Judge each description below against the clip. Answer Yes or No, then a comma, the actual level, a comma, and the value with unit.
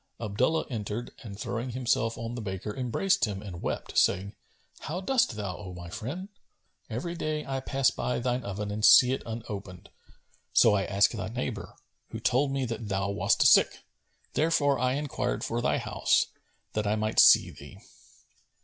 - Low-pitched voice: Yes, low, 115 Hz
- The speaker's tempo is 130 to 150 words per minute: No, average, 170 wpm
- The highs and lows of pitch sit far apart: No, average, 4.3 semitones